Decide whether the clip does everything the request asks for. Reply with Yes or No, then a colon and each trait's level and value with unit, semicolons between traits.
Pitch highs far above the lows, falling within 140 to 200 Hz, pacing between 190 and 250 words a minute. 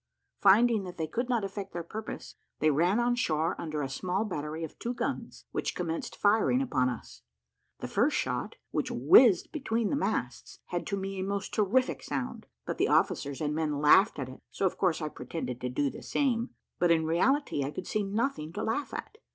Yes: wide, 6.7 semitones; medium, 185 Hz; fast, 205 wpm